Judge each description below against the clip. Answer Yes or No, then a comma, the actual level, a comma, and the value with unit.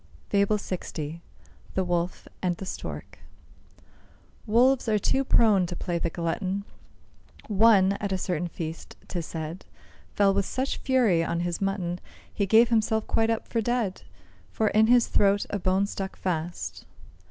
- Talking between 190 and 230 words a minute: No, average, 155 wpm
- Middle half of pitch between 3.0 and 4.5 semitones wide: Yes, average, 3.8 semitones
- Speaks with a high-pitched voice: Yes, high, 195 Hz